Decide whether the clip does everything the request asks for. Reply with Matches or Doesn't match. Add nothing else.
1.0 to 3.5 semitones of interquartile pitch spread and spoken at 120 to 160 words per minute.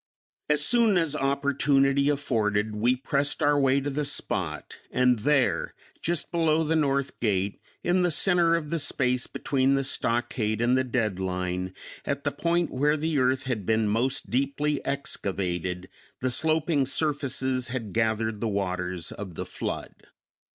Doesn't match